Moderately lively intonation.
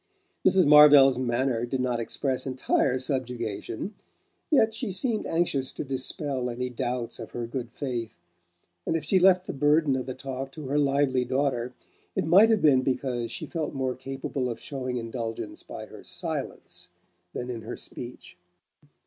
Yes: average, 3.0 semitones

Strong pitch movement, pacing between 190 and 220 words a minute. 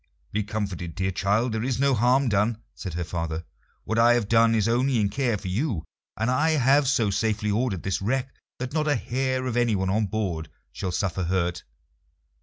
No: average, 4.7 semitones; average, 200 wpm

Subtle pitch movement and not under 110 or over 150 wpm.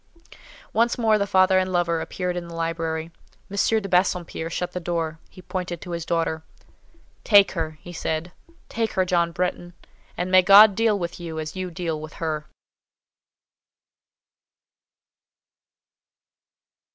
Yes: narrow, 2.2 semitones; average, 140 wpm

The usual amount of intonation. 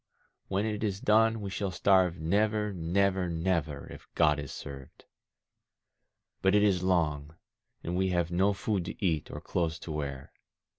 Yes: average, 3.5 semitones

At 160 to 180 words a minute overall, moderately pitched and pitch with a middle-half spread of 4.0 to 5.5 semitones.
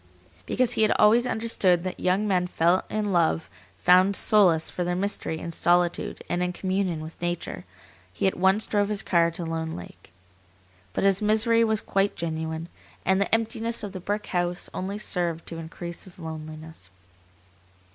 No: average, 165 wpm; medium, 180 Hz; average, 3.6 semitones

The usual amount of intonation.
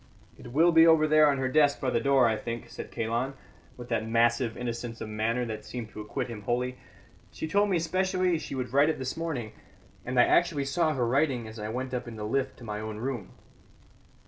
Yes: average, 4.4 semitones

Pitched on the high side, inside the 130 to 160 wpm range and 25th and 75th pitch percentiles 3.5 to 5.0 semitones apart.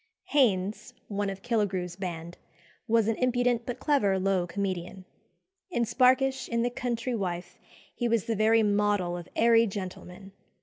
Yes: high, 210 Hz; average, 145 wpm; average, 4.1 semitones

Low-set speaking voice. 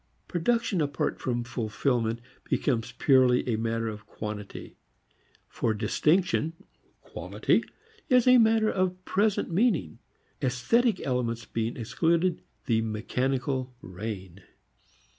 Yes: low, 125 Hz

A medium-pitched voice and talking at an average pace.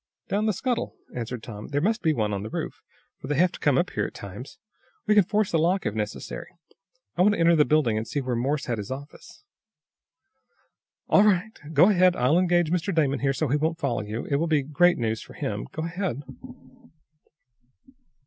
No: medium, 150 Hz; fast, 210 wpm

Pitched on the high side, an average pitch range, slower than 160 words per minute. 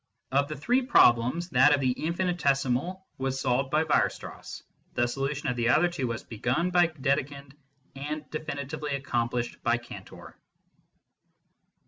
No: medium, 140 Hz; average, 3.7 semitones; average, 140 wpm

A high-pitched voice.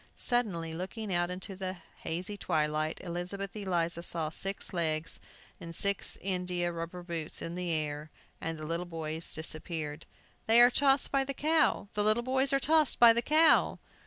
No: medium, 180 Hz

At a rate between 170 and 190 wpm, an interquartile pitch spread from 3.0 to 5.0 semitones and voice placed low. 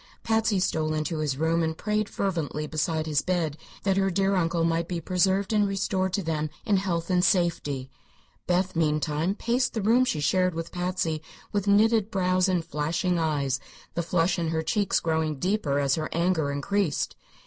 No: average, 180 wpm; average, 3.6 semitones; medium, 175 Hz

